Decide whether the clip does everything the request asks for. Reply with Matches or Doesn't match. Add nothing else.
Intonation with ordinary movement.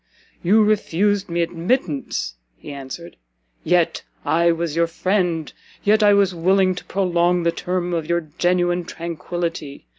Doesn't match